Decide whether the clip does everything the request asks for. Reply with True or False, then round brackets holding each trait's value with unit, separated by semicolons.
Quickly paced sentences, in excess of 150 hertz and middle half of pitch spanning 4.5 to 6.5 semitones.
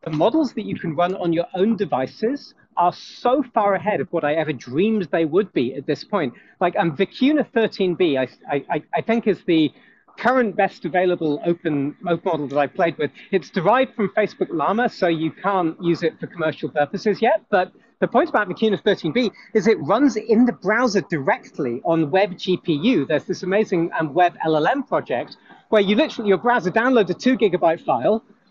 False (190 wpm; 190 Hz; 4.9 semitones)